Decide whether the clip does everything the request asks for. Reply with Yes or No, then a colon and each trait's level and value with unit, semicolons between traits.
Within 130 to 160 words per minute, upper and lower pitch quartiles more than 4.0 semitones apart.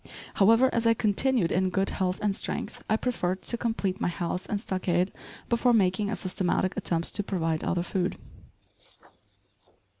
No: average, 155 wpm; average, 3.6 semitones